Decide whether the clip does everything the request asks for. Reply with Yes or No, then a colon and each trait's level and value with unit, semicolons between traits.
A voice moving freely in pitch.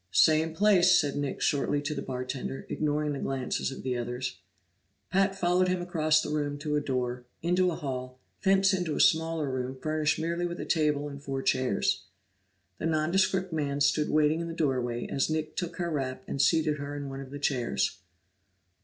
No: average, 3.5 semitones